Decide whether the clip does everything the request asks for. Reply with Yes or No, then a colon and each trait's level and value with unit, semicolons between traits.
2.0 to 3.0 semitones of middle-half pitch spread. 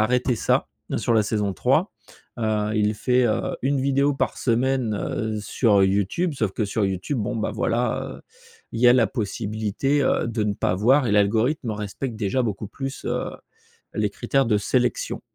No: average, 3.6 semitones